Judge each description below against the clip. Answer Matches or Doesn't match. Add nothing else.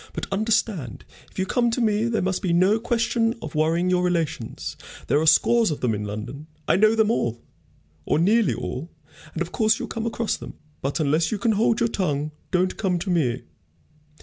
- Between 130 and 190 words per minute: Doesn't match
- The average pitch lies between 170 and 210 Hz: Matches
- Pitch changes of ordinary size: Doesn't match